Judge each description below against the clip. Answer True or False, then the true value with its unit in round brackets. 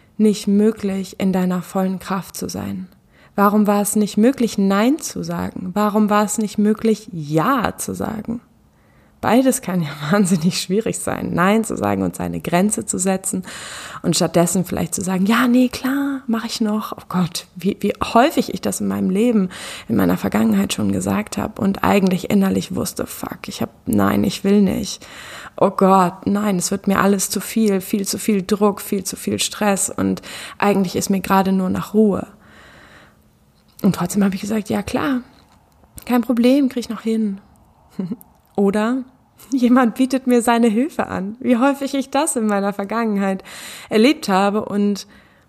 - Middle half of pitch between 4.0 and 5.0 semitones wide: False (3.0 semitones)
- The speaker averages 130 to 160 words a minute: False (175 wpm)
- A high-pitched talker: True (205 Hz)